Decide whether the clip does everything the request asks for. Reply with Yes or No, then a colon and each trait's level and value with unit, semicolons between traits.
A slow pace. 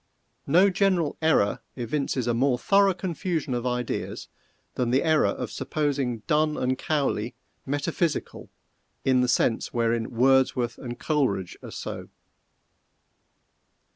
Yes: slow, 120 wpm